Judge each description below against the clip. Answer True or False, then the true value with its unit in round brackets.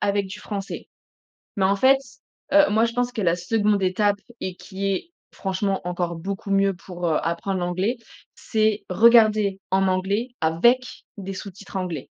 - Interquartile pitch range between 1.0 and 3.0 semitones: True (2.5 semitones)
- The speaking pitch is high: True (195 Hz)